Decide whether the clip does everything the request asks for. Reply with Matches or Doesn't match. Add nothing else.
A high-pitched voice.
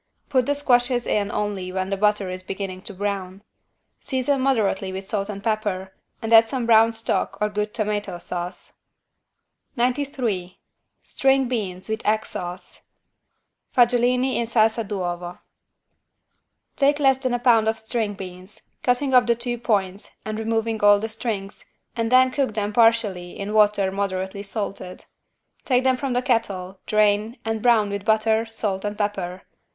Matches